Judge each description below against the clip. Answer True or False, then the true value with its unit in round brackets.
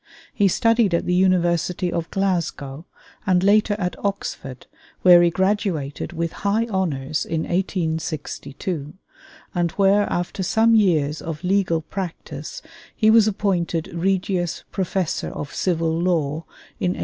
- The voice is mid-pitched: True (180 Hz)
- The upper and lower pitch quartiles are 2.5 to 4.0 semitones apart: True (3.2 semitones)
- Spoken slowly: True (130 wpm)